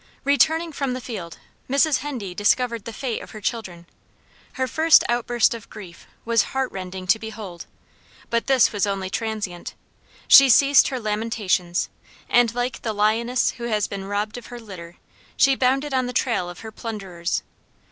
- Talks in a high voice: Yes, high, 225 Hz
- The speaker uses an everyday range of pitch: Yes, average, 4.1 semitones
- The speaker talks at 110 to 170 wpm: Yes, average, 165 wpm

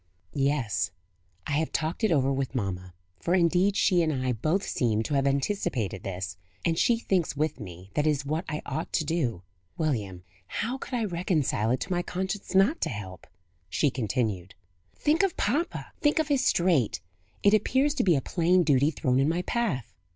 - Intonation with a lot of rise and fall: Yes, wide, 7.3 semitones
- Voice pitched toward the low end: No, medium, 155 Hz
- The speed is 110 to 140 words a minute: No, average, 190 wpm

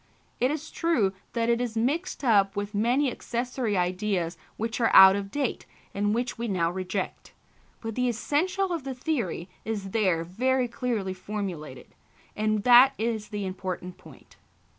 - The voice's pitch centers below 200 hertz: No, high, 220 Hz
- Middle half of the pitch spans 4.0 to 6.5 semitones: Yes, average, 4.5 semitones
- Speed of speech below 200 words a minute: Yes, average, 160 wpm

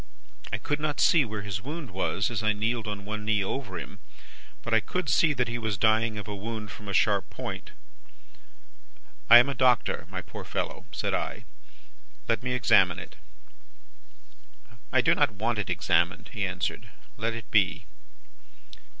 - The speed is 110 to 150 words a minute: No, average, 175 wpm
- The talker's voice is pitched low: Yes, low, 110 Hz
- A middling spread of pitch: Yes, average, 3.0 semitones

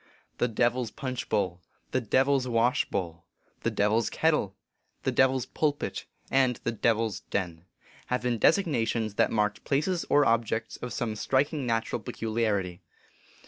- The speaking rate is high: No, average, 185 wpm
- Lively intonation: No, average, 3.6 semitones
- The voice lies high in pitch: No, low, 115 Hz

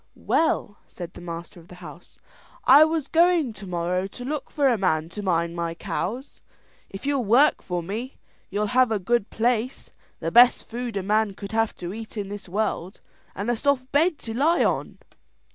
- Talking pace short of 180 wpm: No, average, 190 wpm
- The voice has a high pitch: Yes, high, 215 Hz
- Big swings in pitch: Yes, wide, 5.8 semitones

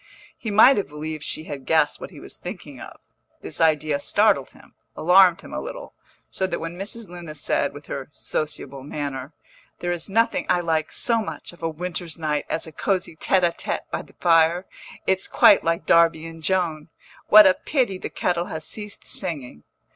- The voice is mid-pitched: Yes, medium, 170 Hz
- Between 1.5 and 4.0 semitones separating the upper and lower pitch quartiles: Yes, average, 3.4 semitones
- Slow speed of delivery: No, average, 190 wpm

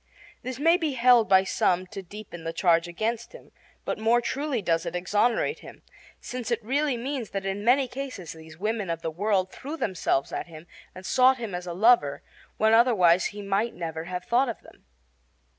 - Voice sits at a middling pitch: No, high, 210 Hz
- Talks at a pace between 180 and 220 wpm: Yes, average, 195 wpm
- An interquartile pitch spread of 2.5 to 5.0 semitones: No, wide, 5.6 semitones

